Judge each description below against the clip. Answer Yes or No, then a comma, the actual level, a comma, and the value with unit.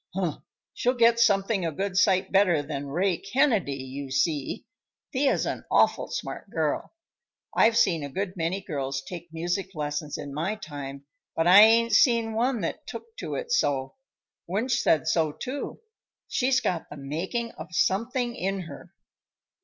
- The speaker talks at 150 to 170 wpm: Yes, average, 160 wpm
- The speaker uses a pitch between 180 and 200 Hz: Yes, medium, 185 Hz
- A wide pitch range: Yes, wide, 7.3 semitones